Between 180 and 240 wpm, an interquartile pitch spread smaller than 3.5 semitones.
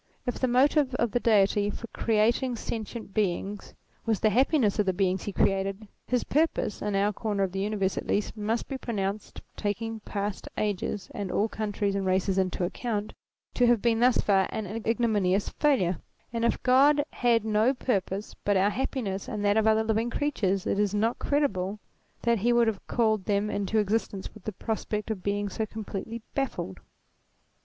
Yes: average, 185 wpm; average, 2.9 semitones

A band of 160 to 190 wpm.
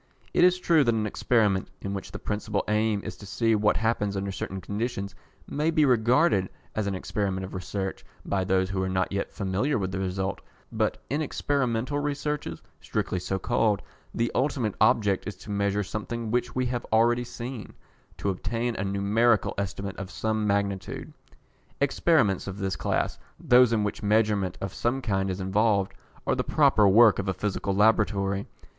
Yes: average, 175 wpm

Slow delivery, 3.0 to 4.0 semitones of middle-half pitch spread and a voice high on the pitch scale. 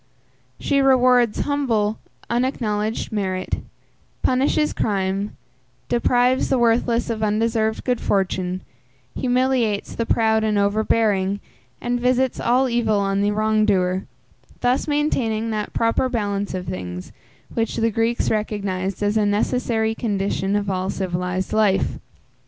Yes: slow, 125 wpm; average, 3.3 semitones; high, 220 Hz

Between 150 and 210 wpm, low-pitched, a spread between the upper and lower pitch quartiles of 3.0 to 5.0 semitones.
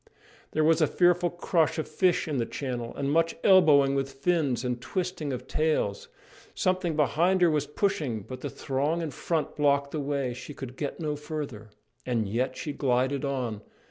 No: average, 180 wpm; medium, 145 Hz; average, 4.0 semitones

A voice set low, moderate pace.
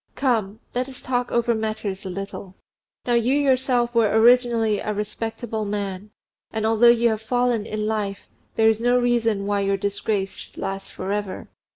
No: high, 220 Hz; average, 175 wpm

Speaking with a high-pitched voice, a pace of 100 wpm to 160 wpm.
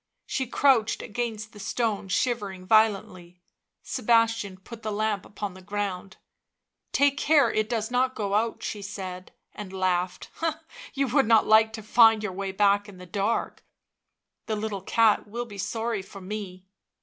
No: high, 210 Hz; average, 170 wpm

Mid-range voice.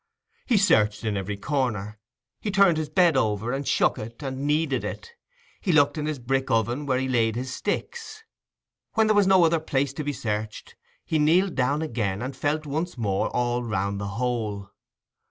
No: low, 130 Hz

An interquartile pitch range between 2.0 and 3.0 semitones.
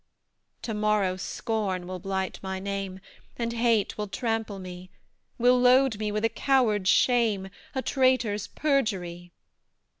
No: average, 3.8 semitones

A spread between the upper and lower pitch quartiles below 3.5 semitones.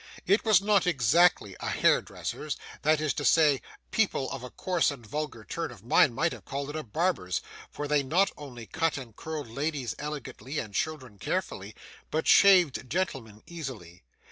No: average, 5.1 semitones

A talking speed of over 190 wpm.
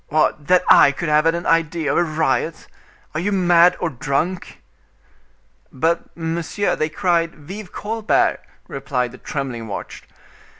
No: average, 145 wpm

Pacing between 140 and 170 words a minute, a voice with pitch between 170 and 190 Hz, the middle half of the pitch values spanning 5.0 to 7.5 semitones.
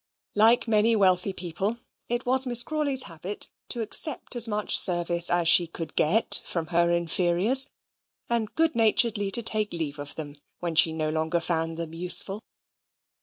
Yes: average, 165 wpm; medium, 185 Hz; wide, 5.4 semitones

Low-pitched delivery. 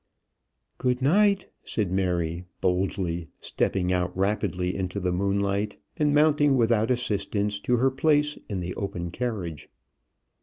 Yes: low, 100 Hz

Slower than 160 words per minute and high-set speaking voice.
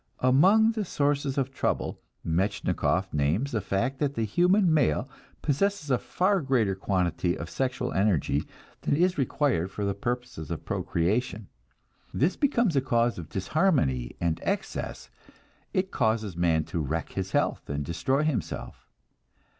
No: average, 140 wpm; low, 120 Hz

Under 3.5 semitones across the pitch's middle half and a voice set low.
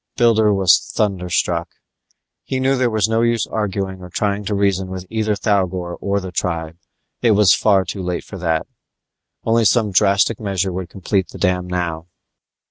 Yes: average, 3.0 semitones; low, 100 Hz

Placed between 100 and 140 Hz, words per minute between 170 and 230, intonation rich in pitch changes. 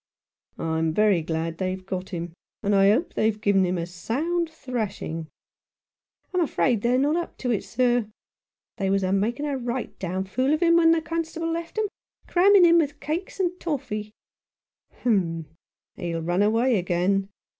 No: high, 220 Hz; average, 175 wpm; wide, 8.6 semitones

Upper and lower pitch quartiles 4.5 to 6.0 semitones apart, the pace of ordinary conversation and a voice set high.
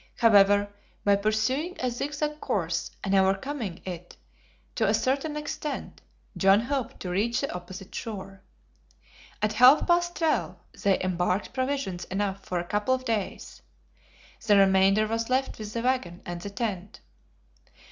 Yes: average, 5.2 semitones; average, 145 wpm; high, 210 Hz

